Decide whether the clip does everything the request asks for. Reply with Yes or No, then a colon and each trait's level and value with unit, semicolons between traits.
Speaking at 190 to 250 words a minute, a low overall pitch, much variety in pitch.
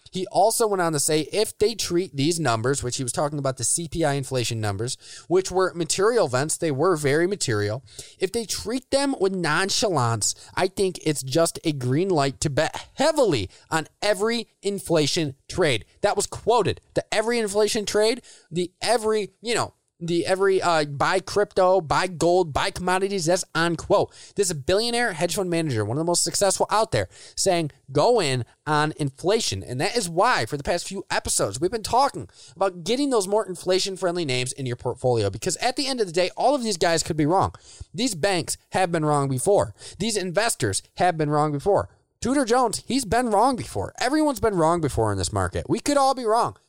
No: average, 200 wpm; medium, 175 Hz; wide, 5.7 semitones